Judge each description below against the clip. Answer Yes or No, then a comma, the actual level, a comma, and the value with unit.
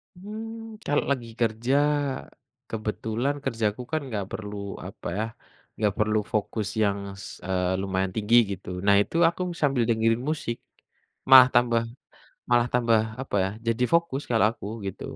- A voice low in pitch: Yes, low, 115 Hz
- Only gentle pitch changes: No, average, 3.8 semitones